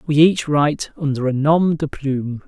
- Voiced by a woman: No, male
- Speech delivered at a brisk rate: No, average, 195 wpm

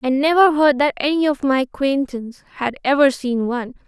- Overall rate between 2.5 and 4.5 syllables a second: No, 5.6 syllables/s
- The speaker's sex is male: No, female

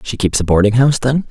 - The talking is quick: Yes, fast, 275 wpm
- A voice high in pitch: No, low, 120 Hz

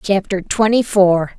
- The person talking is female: Yes, female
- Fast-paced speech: No, slow, 130 wpm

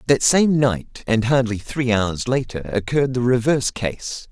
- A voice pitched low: Yes, low, 120 Hz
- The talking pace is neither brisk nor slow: Yes, average, 165 wpm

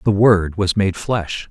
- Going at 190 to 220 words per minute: Yes, average, 200 wpm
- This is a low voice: Yes, low, 100 Hz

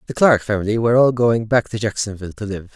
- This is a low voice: Yes, low, 110 Hz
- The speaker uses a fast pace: Yes, fast, 240 wpm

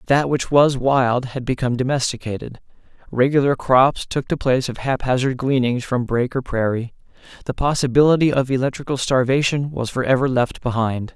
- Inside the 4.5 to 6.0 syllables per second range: Yes, 5.4 syllables/s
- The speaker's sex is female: No, male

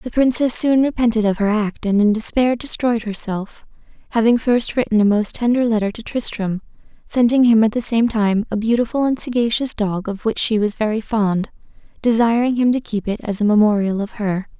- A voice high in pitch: Yes, high, 225 Hz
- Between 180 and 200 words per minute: Yes, average, 195 wpm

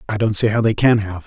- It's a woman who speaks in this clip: No, male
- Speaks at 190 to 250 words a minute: No, fast, 335 wpm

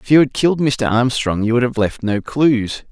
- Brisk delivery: Yes, fast, 245 wpm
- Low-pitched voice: Yes, low, 125 Hz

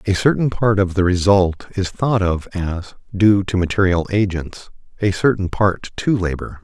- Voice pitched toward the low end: Yes, very low, 95 Hz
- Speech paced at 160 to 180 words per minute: Yes, average, 170 wpm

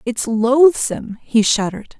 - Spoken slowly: Yes, slow, 120 wpm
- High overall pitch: Yes, high, 235 Hz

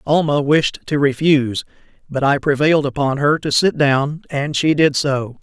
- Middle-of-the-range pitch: Yes, medium, 145 Hz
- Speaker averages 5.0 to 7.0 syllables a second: No, 4.7 syllables/s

